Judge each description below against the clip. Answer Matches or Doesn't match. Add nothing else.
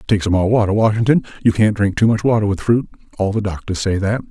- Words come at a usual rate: Doesn't match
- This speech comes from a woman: Doesn't match